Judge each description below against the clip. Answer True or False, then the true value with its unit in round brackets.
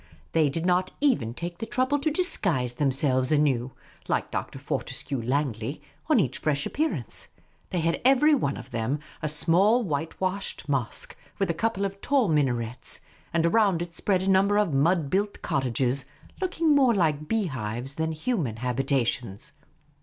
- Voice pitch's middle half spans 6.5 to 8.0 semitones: True (7.0 semitones)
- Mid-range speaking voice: True (160 Hz)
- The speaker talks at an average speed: True (160 wpm)